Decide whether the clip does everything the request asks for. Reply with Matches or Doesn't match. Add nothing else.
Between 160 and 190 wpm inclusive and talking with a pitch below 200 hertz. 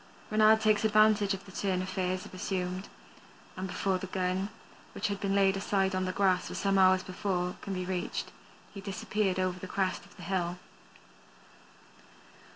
Matches